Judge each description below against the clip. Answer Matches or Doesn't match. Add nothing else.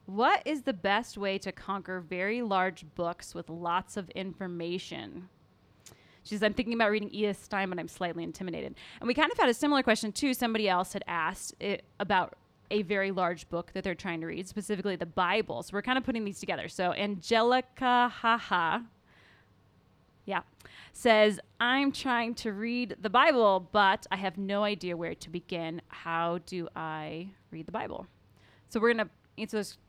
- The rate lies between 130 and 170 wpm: Doesn't match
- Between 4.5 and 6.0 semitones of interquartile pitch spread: Doesn't match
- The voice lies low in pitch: Doesn't match